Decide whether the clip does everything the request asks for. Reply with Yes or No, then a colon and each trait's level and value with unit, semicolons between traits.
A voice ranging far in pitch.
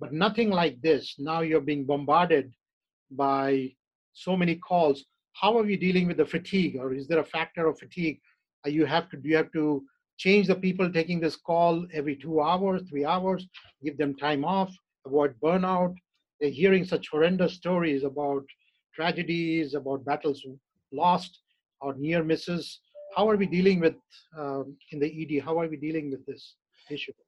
No: average, 3.8 semitones